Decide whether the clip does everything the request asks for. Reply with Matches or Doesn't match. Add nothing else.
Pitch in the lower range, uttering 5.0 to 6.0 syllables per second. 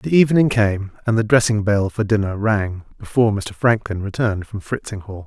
Matches